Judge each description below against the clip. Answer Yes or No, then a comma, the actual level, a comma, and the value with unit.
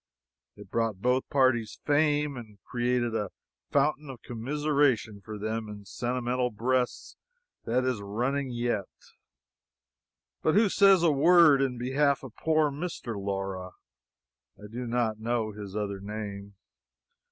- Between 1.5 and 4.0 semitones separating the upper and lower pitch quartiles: No, average, 4.6 semitones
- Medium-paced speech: No, slow, 130 wpm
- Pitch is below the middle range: Yes, low, 120 Hz